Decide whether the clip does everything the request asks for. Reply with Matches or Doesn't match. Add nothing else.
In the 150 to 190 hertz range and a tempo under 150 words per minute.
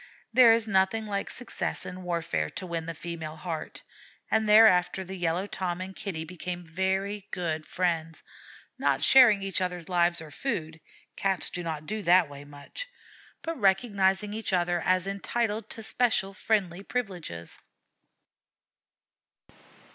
Matches